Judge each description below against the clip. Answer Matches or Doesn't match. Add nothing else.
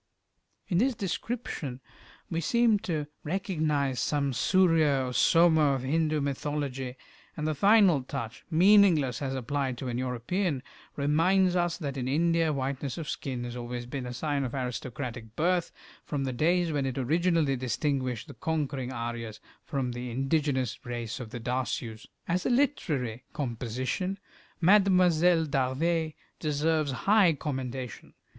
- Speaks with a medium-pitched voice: Matches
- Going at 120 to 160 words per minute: Matches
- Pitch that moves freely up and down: Doesn't match